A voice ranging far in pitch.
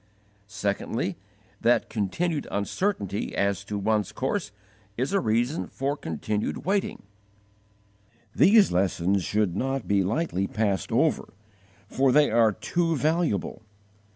Yes: wide, 6.9 semitones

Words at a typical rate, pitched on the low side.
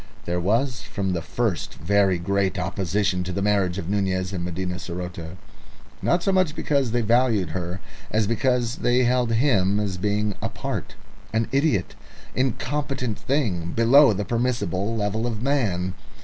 Yes: average, 160 wpm; low, 105 Hz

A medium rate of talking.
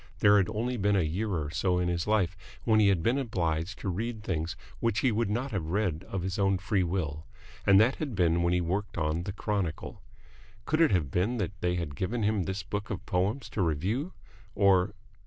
No: fast, 220 wpm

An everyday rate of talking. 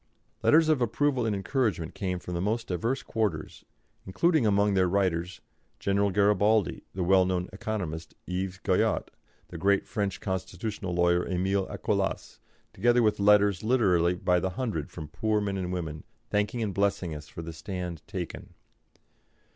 Yes: average, 155 wpm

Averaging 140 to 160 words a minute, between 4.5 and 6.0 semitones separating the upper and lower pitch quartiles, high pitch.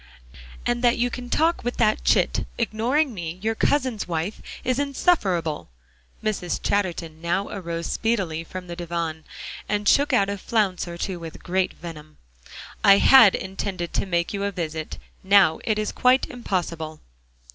Yes: average, 155 wpm; average, 5.2 semitones; high, 195 Hz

